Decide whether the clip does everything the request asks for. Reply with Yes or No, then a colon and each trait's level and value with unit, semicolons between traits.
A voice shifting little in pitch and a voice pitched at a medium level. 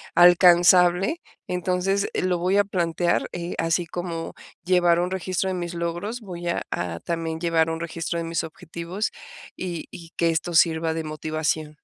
Yes: narrow, 1.5 semitones; medium, 170 Hz